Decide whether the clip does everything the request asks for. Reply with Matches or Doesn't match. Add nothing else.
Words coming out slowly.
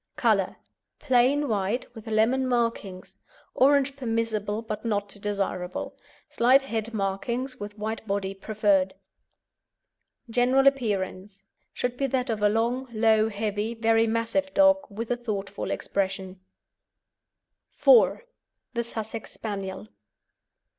Matches